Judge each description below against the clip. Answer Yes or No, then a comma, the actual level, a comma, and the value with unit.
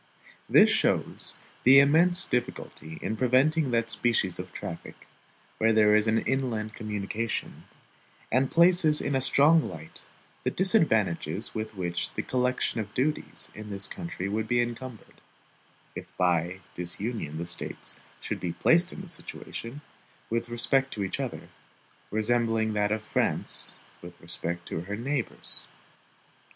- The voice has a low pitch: Yes, low, 115 Hz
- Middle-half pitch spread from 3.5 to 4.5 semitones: No, average, 4.9 semitones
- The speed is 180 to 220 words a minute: No, average, 140 wpm